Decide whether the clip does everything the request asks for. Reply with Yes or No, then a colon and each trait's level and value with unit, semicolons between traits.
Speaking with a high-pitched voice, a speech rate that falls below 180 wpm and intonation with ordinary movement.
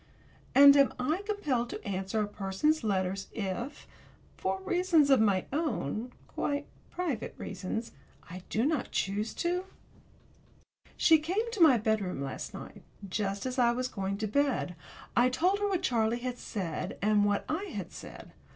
No: high, 240 Hz; average, 160 wpm; wide, 7.3 semitones